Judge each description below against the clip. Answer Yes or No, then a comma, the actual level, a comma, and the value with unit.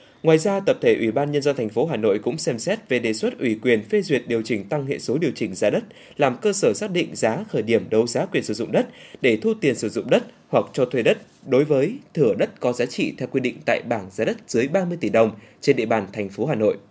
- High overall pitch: No, low, 130 Hz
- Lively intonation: Yes, wide, 6.3 semitones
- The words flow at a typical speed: No, fast, 285 wpm